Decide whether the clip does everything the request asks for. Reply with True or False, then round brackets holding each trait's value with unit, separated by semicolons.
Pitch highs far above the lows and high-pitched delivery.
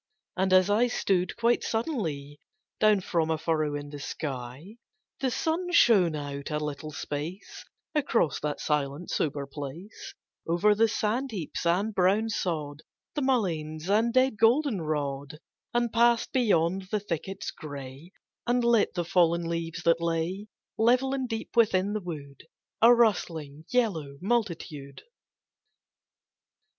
False (6.8 semitones; 180 Hz)